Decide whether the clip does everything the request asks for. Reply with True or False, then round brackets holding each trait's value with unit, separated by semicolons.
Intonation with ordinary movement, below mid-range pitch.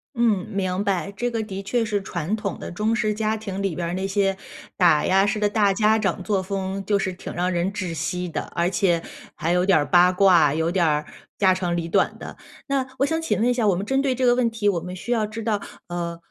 False (3.2 semitones; 195 Hz)